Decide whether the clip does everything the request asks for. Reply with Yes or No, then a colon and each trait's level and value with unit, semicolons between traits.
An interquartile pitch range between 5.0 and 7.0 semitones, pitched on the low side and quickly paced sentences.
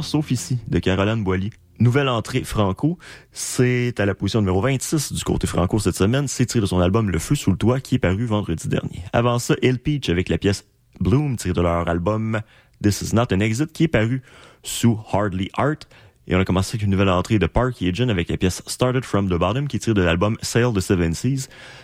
Yes: average, 5.3 semitones; low, 110 Hz; fast, 230 wpm